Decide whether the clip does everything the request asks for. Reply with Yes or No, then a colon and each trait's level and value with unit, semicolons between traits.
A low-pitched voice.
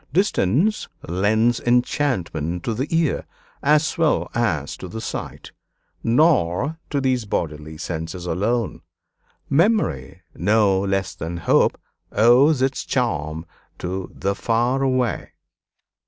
Yes: low, 115 Hz